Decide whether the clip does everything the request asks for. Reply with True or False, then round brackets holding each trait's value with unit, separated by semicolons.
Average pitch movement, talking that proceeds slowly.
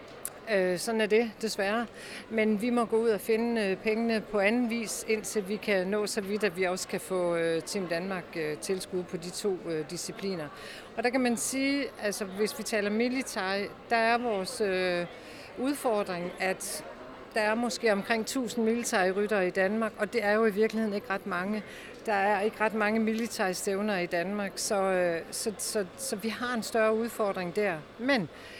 False (3.0 semitones; 180 wpm)